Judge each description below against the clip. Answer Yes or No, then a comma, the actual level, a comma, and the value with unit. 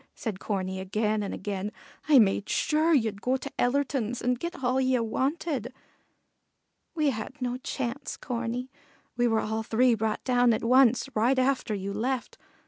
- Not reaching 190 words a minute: Yes, average, 160 wpm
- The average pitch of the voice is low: No, high, 245 Hz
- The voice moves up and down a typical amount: Yes, average, 3.4 semitones